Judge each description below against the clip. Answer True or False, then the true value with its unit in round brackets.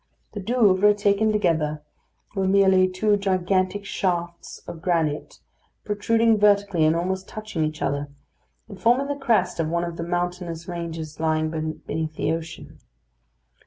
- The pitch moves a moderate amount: True (3.8 semitones)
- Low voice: False (185 Hz)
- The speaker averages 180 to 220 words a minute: False (140 wpm)